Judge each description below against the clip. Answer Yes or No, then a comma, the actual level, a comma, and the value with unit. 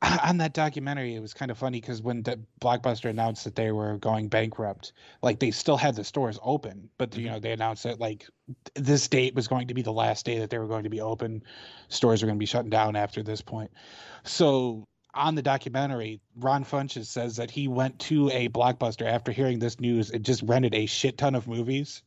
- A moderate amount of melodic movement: Yes, average, 3.0 semitones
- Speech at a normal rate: No, fast, 225 wpm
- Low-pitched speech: Yes, low, 120 Hz